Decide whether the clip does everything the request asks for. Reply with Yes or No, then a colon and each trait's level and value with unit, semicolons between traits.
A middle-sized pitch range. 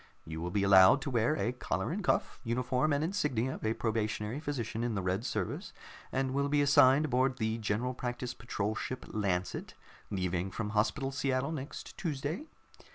Yes: average, 4.6 semitones